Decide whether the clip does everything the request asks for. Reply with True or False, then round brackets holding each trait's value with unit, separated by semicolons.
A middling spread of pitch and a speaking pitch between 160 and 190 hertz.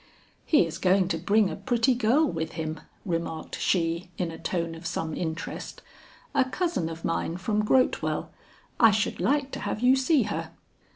False (7.2 semitones; 185 Hz)